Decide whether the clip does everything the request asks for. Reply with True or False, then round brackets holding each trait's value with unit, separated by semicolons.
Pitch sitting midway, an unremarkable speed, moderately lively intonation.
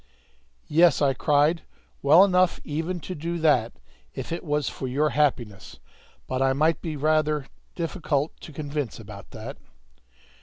True (150 Hz; 145 wpm; 3.1 semitones)